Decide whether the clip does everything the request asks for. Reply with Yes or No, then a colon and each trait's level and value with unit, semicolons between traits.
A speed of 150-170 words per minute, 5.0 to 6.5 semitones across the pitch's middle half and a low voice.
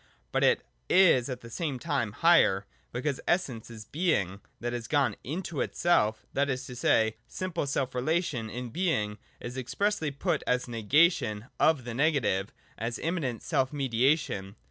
Yes: average, 160 wpm; average, 5.3 semitones; low, 130 Hz